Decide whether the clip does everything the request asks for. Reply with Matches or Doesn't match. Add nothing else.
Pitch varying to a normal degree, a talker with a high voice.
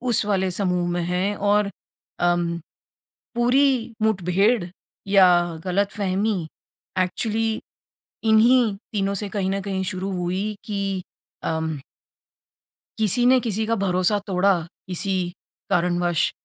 Matches